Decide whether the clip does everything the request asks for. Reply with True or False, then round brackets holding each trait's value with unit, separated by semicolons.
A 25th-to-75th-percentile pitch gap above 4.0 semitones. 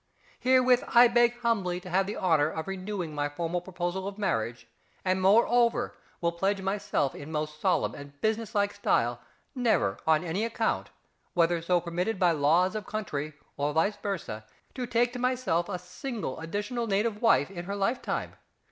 True (5.1 semitones)